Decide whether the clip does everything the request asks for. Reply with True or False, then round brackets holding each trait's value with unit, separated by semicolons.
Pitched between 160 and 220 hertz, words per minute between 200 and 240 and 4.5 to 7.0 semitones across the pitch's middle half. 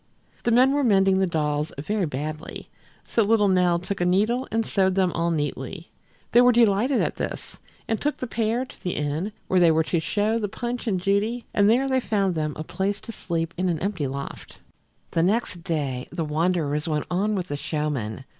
True (185 Hz; 205 wpm; 5.5 semitones)